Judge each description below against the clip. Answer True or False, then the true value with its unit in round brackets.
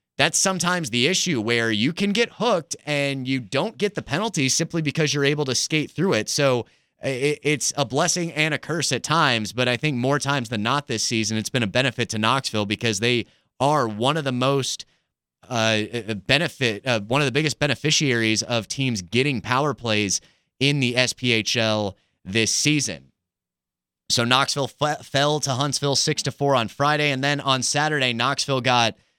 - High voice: False (135 Hz)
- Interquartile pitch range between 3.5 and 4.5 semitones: True (4.1 semitones)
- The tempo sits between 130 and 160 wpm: False (185 wpm)